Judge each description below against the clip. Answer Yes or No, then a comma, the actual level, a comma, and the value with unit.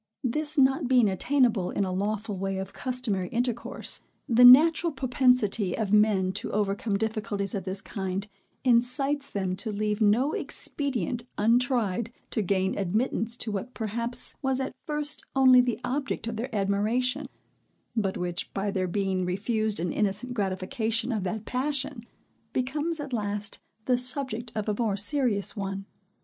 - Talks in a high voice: Yes, high, 220 Hz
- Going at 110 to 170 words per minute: Yes, average, 150 wpm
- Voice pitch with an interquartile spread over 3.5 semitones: Yes, average, 4.1 semitones